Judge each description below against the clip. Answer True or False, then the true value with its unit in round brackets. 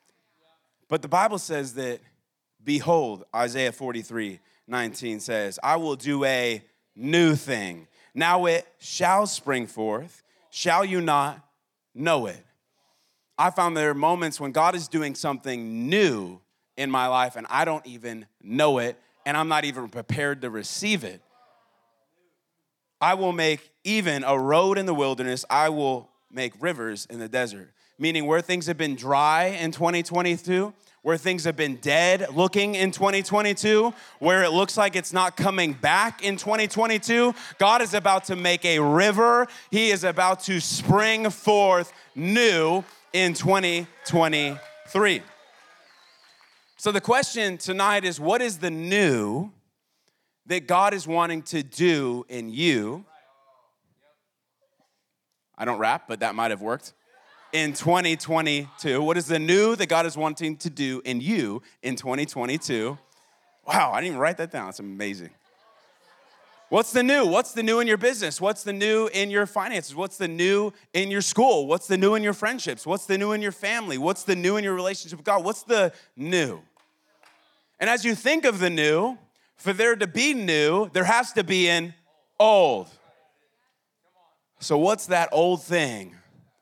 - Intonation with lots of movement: True (5.7 semitones)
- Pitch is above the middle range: False (170 Hz)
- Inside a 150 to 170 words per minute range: True (160 wpm)